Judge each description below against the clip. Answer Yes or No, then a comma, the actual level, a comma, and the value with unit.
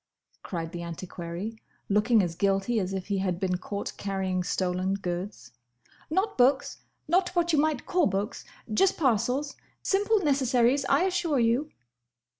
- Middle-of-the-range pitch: No, high, 220 Hz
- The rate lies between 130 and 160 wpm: Yes, average, 145 wpm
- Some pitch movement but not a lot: No, wide, 7.7 semitones